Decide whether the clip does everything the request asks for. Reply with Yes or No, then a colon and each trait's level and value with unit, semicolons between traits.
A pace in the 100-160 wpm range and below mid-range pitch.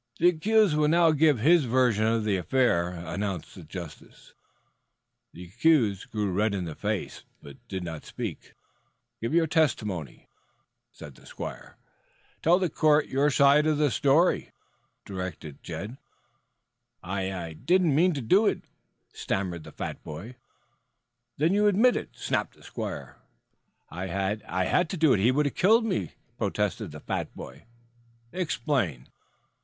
Yes: average, 145 wpm; low, 125 Hz